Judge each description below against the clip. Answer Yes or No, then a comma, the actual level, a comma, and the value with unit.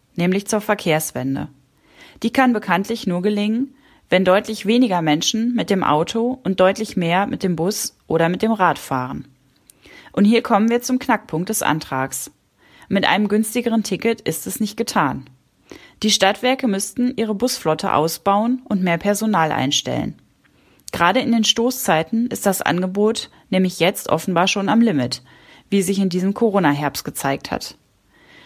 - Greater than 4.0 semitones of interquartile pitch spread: Yes, average, 5.0 semitones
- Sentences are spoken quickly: No, average, 150 wpm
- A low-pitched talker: No, high, 200 Hz